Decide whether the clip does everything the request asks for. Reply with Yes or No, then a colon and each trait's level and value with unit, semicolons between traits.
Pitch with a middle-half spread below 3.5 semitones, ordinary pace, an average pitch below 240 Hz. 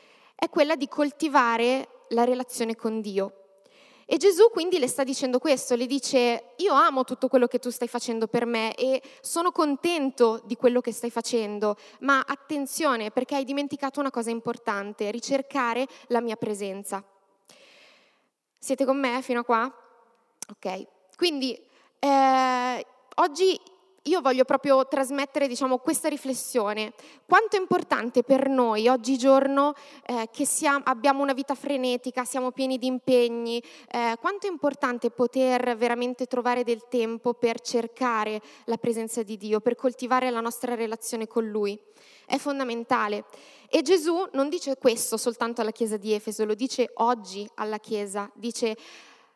No: average, 3.1 semitones; average, 145 wpm; very high, 250 Hz